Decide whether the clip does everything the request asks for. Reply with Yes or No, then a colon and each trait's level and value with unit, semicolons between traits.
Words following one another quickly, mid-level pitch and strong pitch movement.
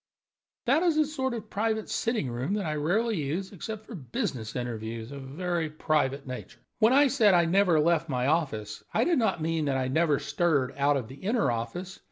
Yes: fast, 210 wpm; medium, 165 Hz; wide, 8.0 semitones